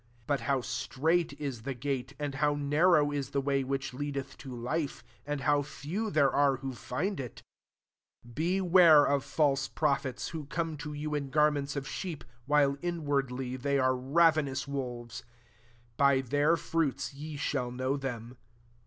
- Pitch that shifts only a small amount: Yes, narrow, 2.2 semitones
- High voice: No, medium, 140 Hz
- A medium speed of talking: Yes, average, 170 wpm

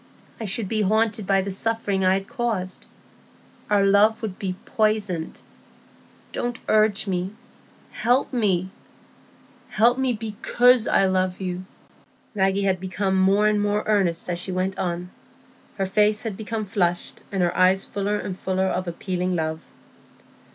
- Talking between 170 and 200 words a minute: No, average, 145 wpm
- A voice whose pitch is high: Yes, high, 195 Hz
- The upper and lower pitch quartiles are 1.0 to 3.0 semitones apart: Yes, narrow, 2.5 semitones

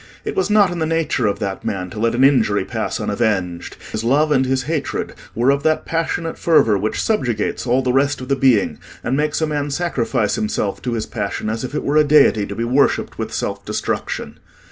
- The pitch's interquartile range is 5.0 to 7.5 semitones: Yes, wide, 5.5 semitones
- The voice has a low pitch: Yes, low, 130 Hz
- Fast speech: Yes, fast, 220 wpm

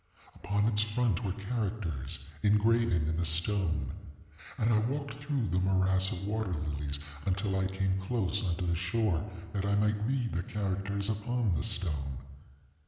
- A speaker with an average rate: Yes, average, 160 wpm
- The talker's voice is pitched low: Yes, low, 100 Hz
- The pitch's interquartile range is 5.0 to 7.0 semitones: No, average, 3.7 semitones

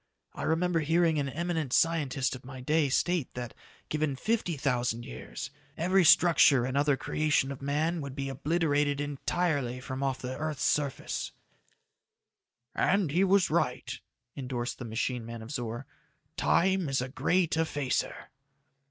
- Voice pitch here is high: No, medium, 145 Hz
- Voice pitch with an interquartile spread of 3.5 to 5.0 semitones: Yes, average, 4.1 semitones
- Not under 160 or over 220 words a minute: No, average, 145 wpm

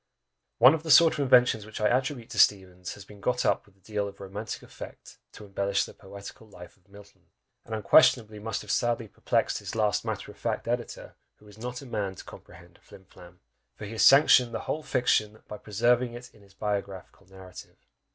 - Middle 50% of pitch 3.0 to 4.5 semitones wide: Yes, average, 3.4 semitones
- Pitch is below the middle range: Yes, low, 105 Hz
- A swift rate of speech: Yes, fast, 210 wpm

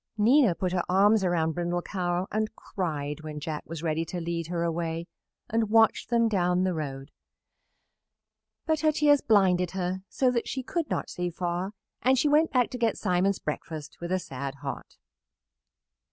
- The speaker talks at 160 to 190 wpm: Yes, average, 170 wpm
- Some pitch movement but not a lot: Yes, average, 4.9 semitones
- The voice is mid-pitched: Yes, medium, 180 Hz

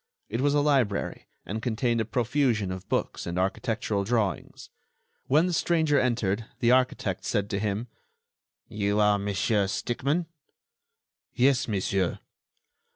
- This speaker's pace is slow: Yes, slow, 130 wpm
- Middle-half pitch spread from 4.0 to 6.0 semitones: Yes, average, 4.3 semitones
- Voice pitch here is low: Yes, low, 110 Hz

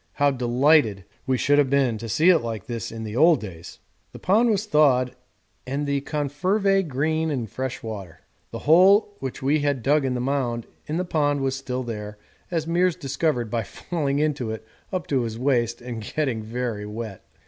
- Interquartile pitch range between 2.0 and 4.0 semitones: No, average, 4.6 semitones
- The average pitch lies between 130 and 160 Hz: Yes, low, 135 Hz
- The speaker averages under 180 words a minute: No, average, 190 wpm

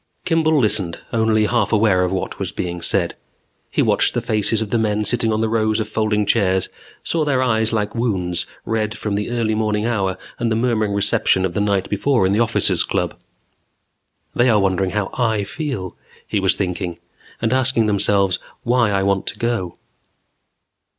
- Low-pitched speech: Yes, low, 110 Hz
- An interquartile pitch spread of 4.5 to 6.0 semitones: No, average, 2.9 semitones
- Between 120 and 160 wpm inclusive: No, average, 185 wpm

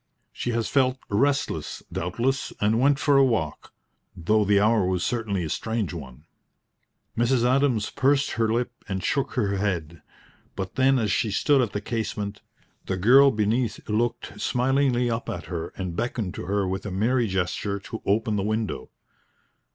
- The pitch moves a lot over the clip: No, average, 4.1 semitones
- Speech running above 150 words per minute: Yes, average, 165 wpm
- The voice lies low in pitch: Yes, low, 110 Hz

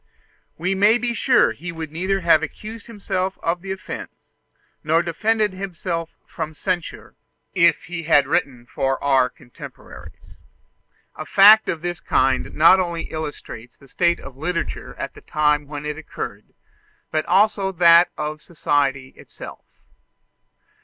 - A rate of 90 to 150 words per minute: Yes, average, 145 wpm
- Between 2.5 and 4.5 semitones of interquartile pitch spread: Yes, average, 4.1 semitones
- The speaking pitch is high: No, medium, 170 Hz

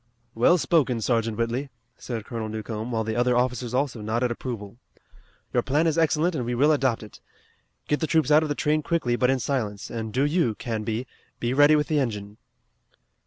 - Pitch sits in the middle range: No, low, 125 Hz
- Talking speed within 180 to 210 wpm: Yes, average, 195 wpm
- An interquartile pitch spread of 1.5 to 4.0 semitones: No, average, 4.5 semitones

